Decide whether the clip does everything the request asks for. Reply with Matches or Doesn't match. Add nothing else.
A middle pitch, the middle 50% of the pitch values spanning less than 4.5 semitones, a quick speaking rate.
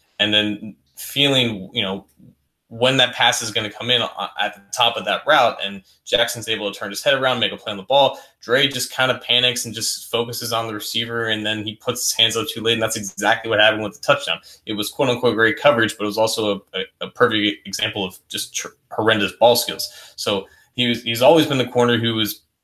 Doesn't match